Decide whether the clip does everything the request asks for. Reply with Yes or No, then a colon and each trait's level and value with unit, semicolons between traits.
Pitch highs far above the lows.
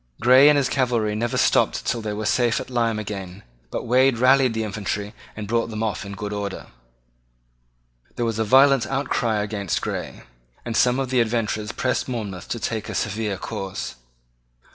No: average, 3.2 semitones